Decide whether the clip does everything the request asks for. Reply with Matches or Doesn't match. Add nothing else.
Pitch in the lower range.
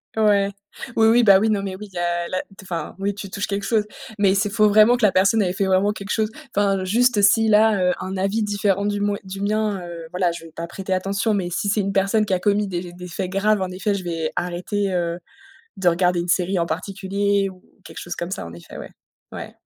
Doesn't match